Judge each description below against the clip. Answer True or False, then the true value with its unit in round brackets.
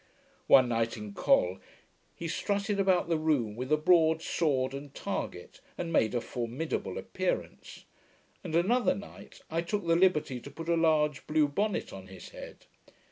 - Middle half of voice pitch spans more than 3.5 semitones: True (5.2 semitones)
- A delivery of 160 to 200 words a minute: True (165 wpm)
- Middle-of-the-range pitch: True (155 Hz)